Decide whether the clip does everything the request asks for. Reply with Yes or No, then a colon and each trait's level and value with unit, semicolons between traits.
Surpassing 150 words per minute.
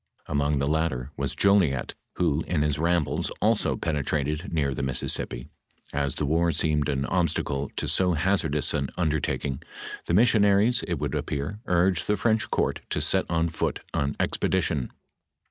Yes: average, 160 wpm